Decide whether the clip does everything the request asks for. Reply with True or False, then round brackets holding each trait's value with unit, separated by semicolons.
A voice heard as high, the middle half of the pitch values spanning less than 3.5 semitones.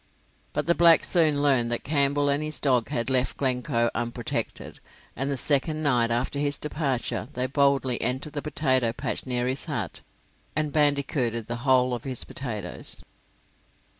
False (135 Hz; 2.9 semitones)